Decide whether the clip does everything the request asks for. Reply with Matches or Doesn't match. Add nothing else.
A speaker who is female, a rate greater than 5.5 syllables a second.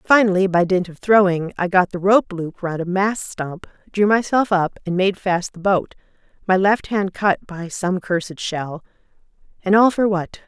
Doesn't match